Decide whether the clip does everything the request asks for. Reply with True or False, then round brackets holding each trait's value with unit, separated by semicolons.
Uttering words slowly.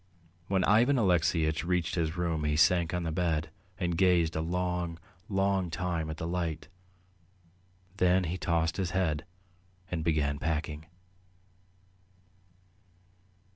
True (125 wpm)